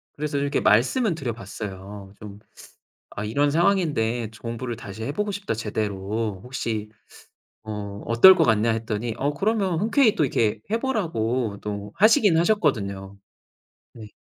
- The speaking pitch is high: No, low, 115 Hz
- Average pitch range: No, wide, 7.6 semitones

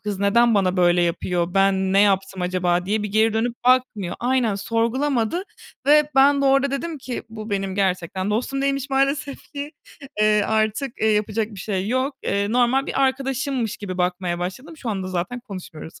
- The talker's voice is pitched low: No, high, 215 Hz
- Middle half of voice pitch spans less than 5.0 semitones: No, wide, 5.5 semitones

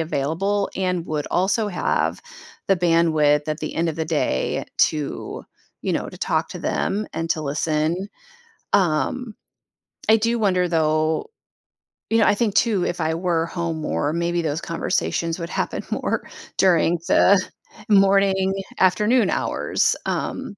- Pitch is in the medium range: Yes, medium, 170 Hz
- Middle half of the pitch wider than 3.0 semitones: Yes, average, 3.6 semitones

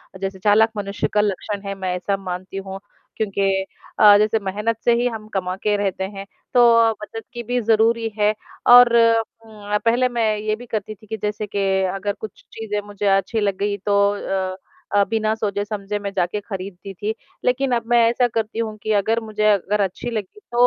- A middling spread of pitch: No, narrow, 2.1 semitones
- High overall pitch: Yes, high, 210 Hz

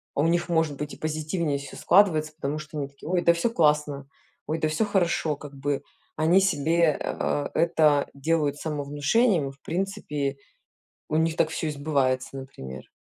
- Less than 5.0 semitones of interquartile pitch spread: Yes, average, 2.7 semitones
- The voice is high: No, medium, 155 Hz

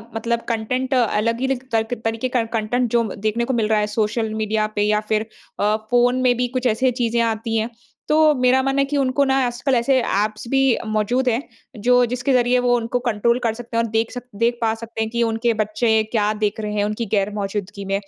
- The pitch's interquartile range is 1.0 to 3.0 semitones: Yes, narrow, 2.4 semitones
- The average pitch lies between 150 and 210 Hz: No, high, 230 Hz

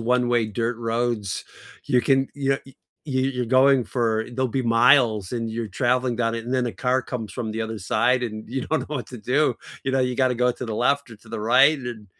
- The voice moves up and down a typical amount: No, narrow, 2.3 semitones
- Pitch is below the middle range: Yes, low, 120 Hz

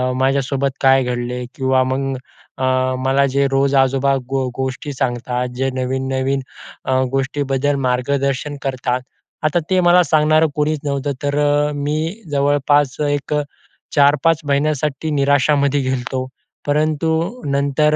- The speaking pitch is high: No, medium, 140 Hz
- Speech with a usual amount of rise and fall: No, narrow, 1.8 semitones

